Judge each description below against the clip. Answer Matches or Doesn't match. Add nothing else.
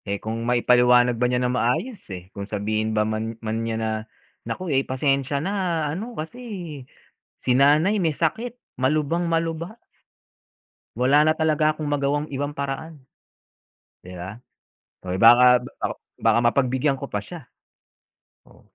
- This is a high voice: Doesn't match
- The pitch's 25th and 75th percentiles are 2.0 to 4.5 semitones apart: Doesn't match